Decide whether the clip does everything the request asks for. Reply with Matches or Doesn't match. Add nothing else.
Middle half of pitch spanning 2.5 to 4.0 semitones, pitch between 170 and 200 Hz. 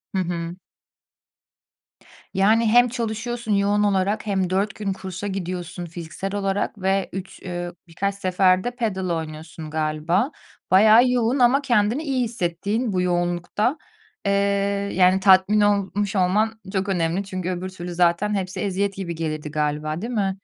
Matches